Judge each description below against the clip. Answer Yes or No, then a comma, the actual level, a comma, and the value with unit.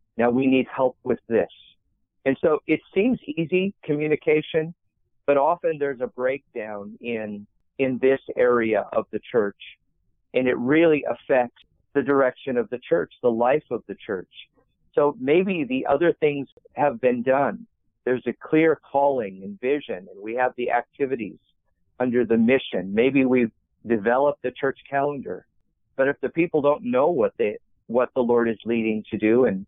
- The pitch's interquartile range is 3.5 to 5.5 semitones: Yes, average, 4.3 semitones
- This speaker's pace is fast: No, average, 165 wpm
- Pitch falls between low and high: No, low, 130 Hz